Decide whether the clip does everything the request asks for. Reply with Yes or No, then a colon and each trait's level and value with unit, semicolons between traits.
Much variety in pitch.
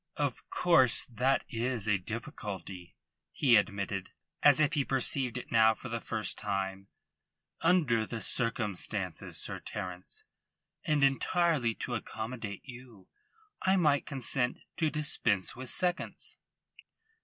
No: average, 4.8 semitones